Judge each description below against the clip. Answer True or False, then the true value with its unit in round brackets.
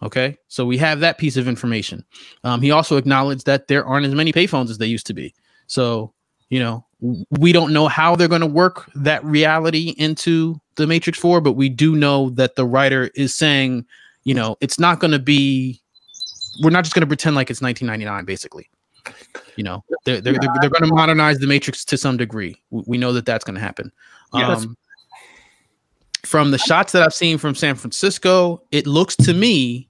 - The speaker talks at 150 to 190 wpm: False (200 wpm)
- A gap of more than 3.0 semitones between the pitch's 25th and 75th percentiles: True (4.3 semitones)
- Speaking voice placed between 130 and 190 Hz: True (140 Hz)